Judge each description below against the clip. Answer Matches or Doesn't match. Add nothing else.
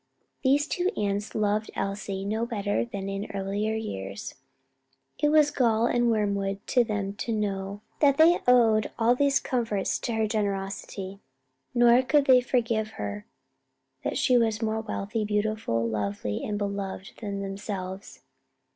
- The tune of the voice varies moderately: Matches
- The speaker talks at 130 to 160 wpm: Matches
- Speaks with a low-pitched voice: Doesn't match